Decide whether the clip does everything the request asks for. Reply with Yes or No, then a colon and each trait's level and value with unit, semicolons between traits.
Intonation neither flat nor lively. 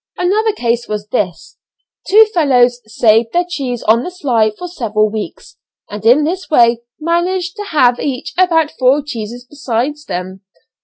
No: wide, 7.2 semitones